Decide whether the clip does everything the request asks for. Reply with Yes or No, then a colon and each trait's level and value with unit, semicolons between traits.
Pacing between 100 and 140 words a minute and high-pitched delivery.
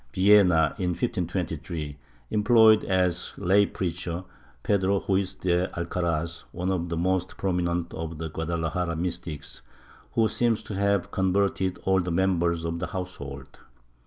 No: slow, 135 wpm; very low, 90 Hz